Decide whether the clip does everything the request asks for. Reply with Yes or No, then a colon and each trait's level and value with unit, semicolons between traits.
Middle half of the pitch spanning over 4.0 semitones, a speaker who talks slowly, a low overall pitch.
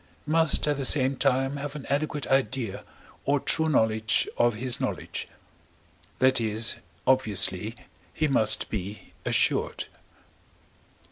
Yes: average, 4.4 semitones; slow, 120 wpm; low, 130 Hz